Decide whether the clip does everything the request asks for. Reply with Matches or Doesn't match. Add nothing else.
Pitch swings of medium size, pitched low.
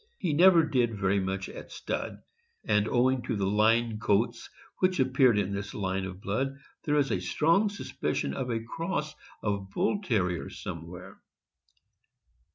Doesn't match